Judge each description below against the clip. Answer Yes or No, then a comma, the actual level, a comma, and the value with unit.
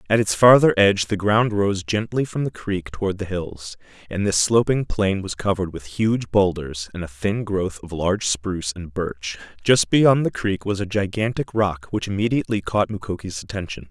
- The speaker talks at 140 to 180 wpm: No, average, 195 wpm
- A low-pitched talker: Yes, low, 100 Hz